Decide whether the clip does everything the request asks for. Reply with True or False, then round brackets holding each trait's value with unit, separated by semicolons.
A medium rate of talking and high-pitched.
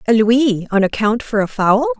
False (210 wpm; 220 Hz)